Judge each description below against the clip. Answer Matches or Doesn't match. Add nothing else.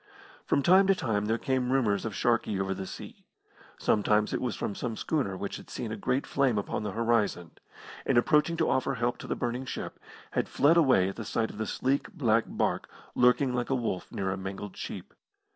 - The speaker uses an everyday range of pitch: Matches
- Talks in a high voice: Doesn't match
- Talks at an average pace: Doesn't match